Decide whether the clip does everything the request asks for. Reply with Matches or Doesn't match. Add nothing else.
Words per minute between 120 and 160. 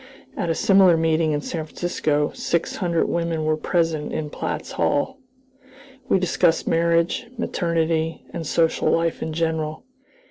Matches